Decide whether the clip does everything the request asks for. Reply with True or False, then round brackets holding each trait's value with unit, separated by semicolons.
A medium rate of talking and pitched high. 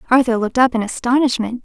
True (185 wpm; 240 Hz)